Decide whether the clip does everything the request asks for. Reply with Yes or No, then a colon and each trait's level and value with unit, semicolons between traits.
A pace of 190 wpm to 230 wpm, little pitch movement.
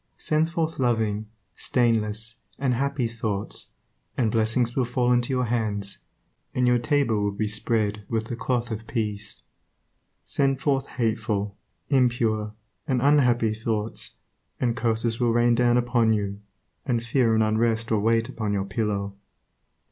No: average, 145 wpm; narrow, 2.3 semitones